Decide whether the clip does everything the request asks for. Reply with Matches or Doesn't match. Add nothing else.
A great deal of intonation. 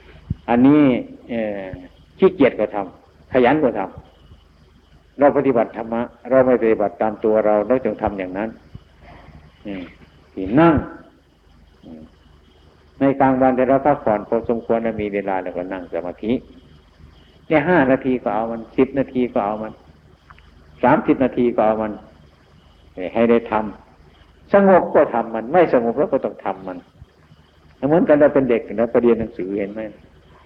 Matches